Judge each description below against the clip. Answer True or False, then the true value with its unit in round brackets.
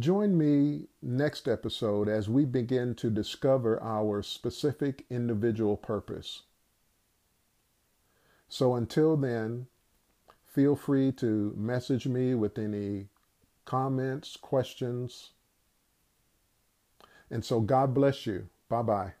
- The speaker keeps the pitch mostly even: False (3.7 semitones)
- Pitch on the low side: True (120 Hz)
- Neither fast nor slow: False (100 wpm)